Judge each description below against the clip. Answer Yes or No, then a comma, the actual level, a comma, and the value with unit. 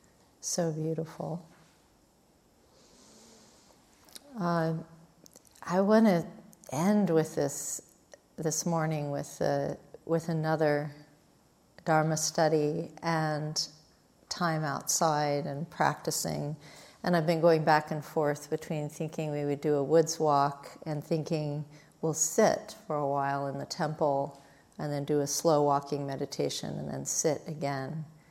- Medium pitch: Yes, medium, 155 Hz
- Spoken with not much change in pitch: Yes, narrow, 2.1 semitones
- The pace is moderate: No, slow, 125 wpm